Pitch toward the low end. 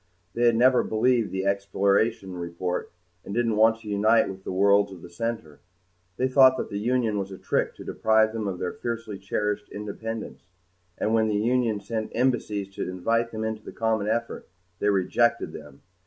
Yes: low, 110 Hz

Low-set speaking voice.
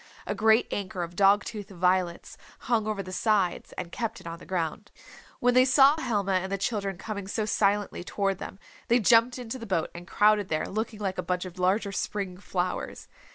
No: high, 200 Hz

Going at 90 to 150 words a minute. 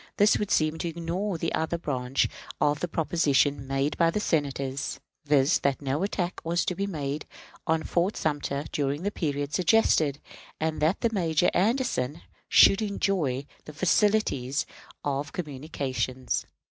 Yes: average, 145 wpm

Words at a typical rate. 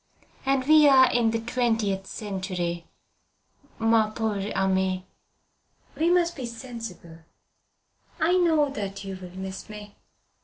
No: slow, 120 wpm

